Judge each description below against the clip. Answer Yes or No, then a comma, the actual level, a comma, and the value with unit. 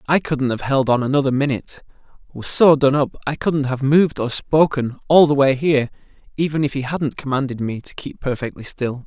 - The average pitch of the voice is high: No, medium, 140 Hz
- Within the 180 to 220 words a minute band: Yes, average, 200 wpm